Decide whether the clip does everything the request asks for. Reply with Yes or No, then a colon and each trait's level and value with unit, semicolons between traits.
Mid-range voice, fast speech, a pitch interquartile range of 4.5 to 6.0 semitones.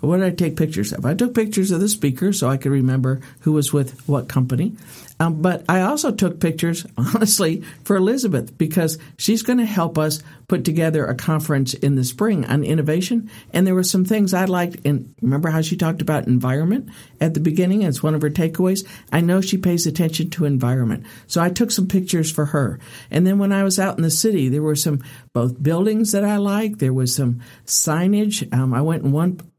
Yes: medium, 165 Hz; fast, 215 wpm; average, 5.1 semitones